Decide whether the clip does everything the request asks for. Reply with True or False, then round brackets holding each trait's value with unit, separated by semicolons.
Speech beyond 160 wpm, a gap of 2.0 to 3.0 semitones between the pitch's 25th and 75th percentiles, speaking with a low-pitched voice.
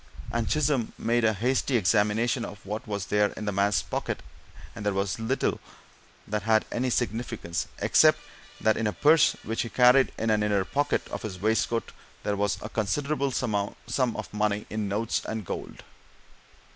True (170 wpm; 2.6 semitones; 110 Hz)